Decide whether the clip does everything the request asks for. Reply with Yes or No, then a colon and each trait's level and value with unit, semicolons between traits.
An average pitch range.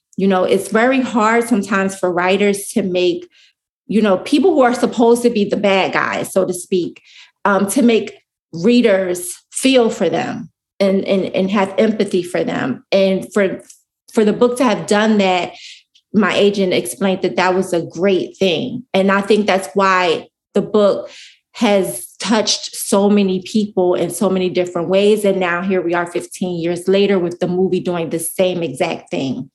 Yes: average, 3.0 semitones